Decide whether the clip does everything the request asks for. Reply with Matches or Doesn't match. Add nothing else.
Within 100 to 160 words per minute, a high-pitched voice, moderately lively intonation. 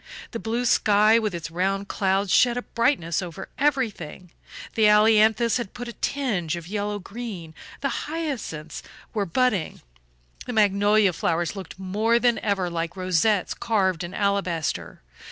Matches